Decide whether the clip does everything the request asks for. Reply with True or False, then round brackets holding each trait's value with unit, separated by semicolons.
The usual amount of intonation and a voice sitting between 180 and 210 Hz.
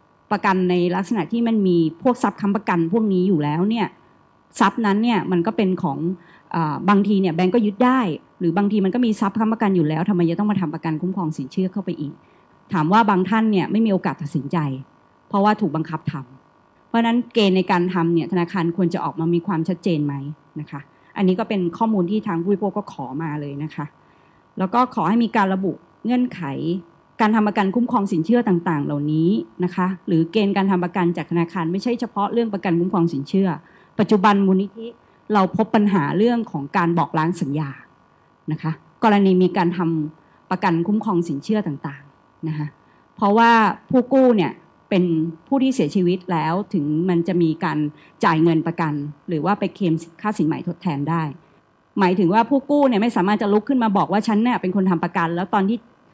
True (4.2 semitones; 185 Hz)